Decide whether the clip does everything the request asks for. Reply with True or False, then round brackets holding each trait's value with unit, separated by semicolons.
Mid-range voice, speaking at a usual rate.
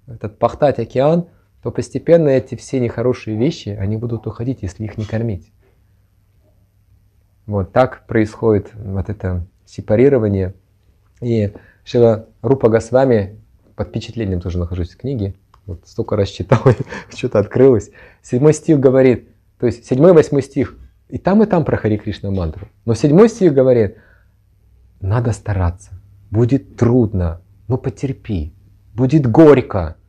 False (110 Hz; 130 wpm)